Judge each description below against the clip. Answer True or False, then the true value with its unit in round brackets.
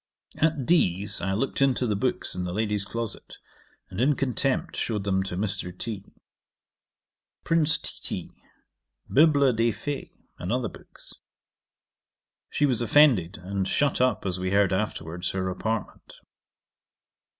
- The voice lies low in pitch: True (110 Hz)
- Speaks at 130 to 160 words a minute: True (140 wpm)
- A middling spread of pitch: False (5.9 semitones)